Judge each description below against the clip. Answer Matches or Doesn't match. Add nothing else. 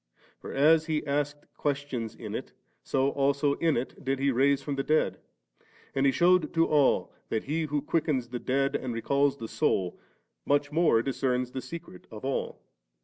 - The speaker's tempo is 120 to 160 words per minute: Doesn't match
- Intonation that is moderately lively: Doesn't match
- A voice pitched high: Doesn't match